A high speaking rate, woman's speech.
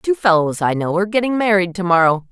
Yes: fast, 235 wpm; female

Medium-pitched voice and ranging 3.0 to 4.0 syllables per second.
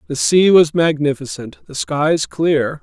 Yes: medium, 155 Hz; 3.9 syllables/s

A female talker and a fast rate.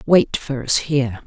No: female; average, 190 wpm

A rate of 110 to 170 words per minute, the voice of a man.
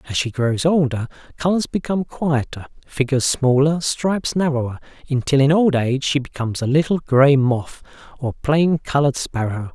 Yes: average, 155 wpm; male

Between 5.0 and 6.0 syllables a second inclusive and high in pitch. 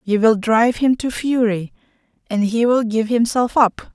No: 4.5 syllables/s; high, 230 Hz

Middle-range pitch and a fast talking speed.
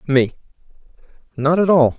No: medium, 150 Hz; slow, 120 wpm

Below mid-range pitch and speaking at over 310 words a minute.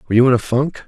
Yes: low, 125 Hz; fast, 340 wpm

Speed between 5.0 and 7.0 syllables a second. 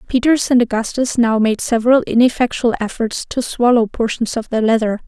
Yes: 5.4 syllables/s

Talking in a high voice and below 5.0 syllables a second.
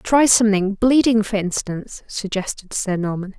Yes: high, 210 Hz; 4.8 syllables/s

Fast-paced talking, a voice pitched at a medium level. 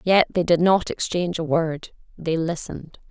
No: average, 175 wpm; medium, 170 Hz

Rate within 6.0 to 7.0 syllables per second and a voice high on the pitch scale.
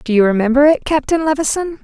Yes: 6.2 syllables/s; very high, 280 Hz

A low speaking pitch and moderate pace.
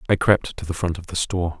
No: very low, 85 Hz; fast, 300 wpm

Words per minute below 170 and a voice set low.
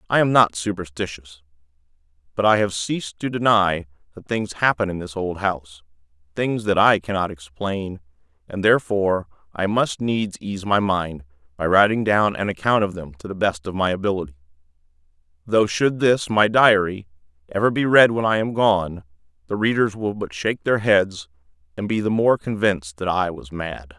No: average, 175 wpm; very low, 95 Hz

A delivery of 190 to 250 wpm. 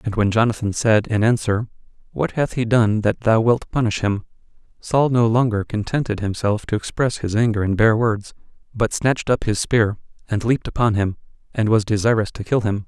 Yes: average, 195 wpm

